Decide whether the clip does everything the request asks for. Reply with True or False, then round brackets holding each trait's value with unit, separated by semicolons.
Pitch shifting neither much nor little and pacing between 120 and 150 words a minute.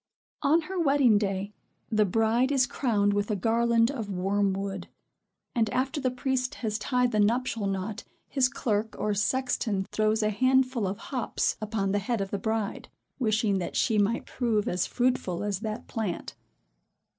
False (3.6 semitones; 165 wpm)